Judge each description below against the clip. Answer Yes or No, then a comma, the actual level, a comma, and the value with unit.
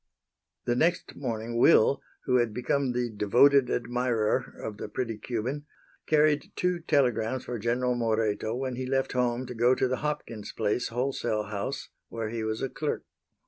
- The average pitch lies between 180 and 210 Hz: No, low, 125 Hz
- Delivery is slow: No, average, 165 wpm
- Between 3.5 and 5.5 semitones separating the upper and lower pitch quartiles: No, average, 2.7 semitones